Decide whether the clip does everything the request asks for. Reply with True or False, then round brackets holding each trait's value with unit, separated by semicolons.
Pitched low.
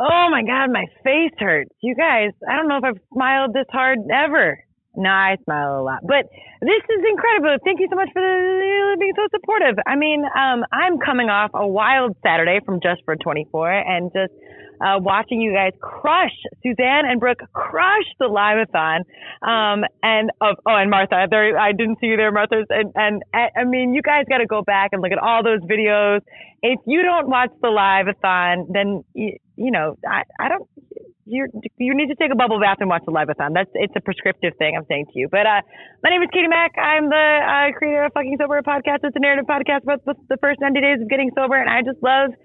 False (250 Hz)